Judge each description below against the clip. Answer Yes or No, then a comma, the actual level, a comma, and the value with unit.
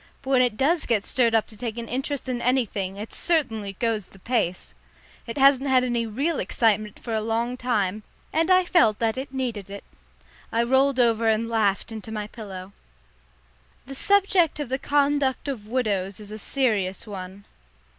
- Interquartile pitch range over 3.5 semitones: Yes, average, 3.9 semitones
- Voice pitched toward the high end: Yes, high, 230 Hz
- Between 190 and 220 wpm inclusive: No, average, 180 wpm